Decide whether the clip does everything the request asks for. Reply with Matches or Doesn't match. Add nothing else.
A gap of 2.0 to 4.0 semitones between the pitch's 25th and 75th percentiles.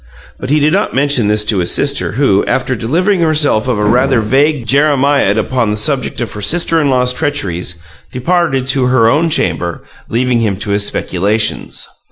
Doesn't match